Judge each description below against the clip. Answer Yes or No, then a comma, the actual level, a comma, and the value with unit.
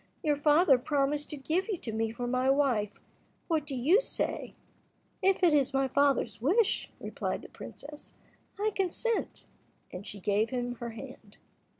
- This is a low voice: No, very high, 280 Hz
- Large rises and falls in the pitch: No, average, 4.7 semitones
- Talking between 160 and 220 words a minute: Yes, average, 165 wpm